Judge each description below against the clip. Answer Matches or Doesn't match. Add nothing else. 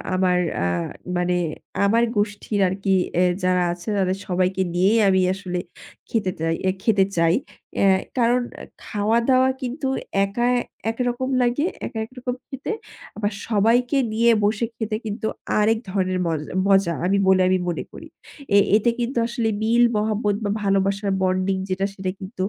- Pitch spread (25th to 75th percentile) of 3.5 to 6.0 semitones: Matches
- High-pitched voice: Matches